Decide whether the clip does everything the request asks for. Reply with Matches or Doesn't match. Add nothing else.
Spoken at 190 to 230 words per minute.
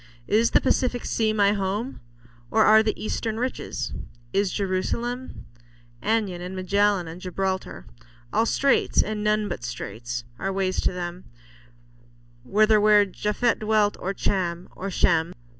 Doesn't match